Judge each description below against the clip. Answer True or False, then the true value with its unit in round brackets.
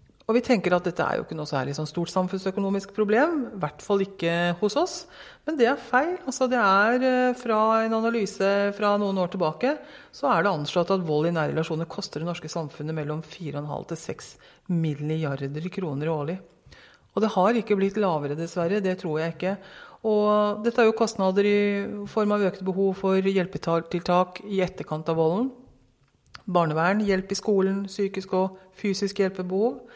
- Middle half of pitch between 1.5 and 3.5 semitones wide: False (4.0 semitones)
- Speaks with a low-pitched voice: False (190 Hz)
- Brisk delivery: False (180 wpm)